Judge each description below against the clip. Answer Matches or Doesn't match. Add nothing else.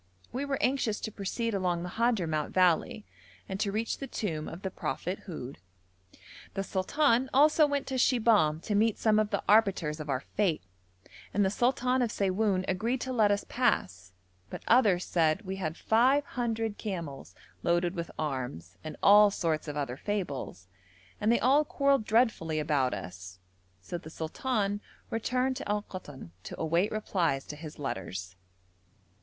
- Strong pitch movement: Matches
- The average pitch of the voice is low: Doesn't match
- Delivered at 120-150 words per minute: Doesn't match